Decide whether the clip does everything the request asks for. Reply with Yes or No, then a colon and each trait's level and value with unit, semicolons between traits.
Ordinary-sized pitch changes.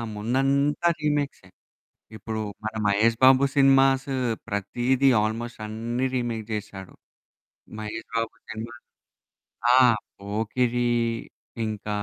Yes: average, 3.5 semitones